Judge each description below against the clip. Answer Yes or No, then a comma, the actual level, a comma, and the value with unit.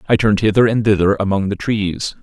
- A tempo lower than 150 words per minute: No, fast, 215 wpm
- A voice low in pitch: Yes, low, 105 Hz